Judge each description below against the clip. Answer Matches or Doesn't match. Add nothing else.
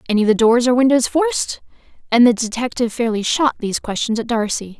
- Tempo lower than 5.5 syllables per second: Doesn't match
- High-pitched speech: Matches